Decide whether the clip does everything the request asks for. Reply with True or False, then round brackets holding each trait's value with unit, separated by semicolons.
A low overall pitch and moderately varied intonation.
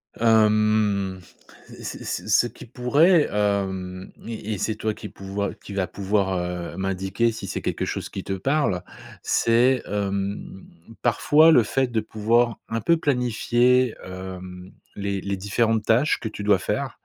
True (105 Hz; 3.4 semitones)